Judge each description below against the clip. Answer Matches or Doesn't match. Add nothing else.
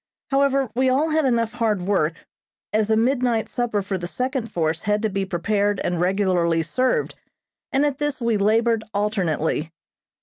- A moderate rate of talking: Matches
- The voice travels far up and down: Doesn't match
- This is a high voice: Matches